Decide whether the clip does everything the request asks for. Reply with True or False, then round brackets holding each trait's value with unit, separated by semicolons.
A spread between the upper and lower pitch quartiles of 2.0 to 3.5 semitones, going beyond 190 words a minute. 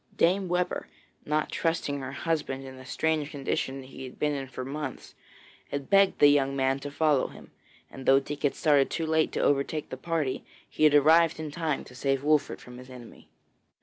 True (2.8 semitones; 200 wpm)